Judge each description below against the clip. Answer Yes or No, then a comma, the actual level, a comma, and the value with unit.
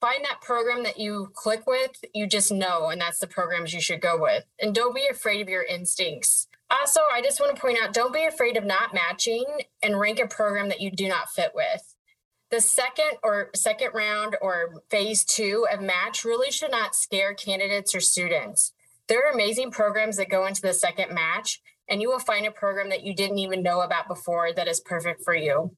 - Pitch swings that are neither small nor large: Yes, average, 4.6 semitones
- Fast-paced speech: Yes, fast, 215 wpm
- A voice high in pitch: Yes, high, 210 Hz